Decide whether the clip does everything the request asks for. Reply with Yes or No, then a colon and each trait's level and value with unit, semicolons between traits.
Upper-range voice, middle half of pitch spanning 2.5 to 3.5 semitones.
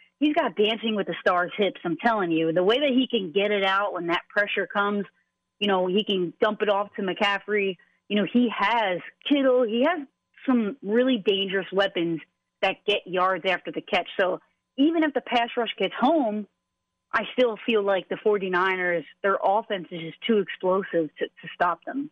No: high, 205 Hz; average, 3.9 semitones